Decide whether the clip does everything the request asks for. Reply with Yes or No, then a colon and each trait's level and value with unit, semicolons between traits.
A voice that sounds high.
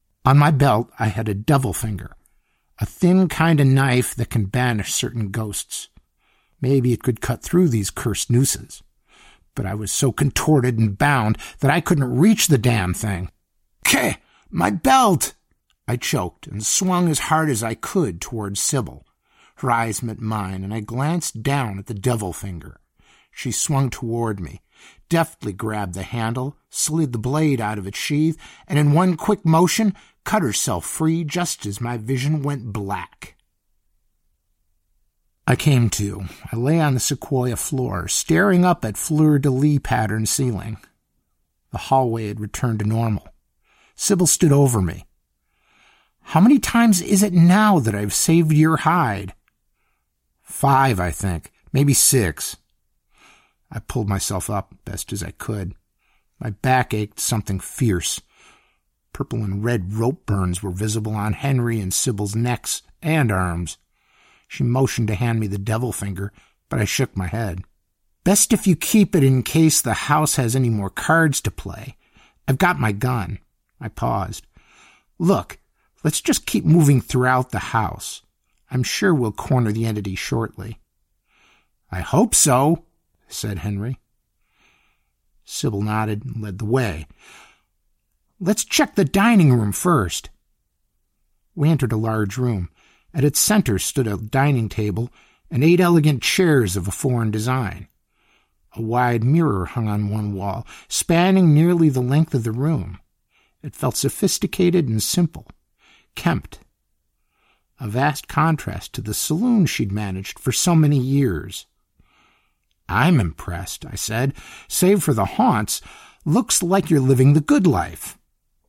No: low, 120 Hz